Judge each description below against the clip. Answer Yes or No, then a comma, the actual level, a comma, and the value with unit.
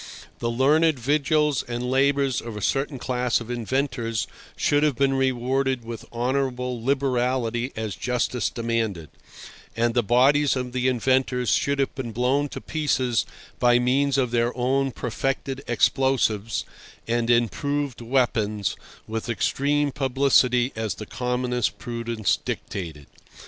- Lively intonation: No, narrow, 2.5 semitones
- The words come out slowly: Yes, slow, 130 wpm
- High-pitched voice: No, low, 125 Hz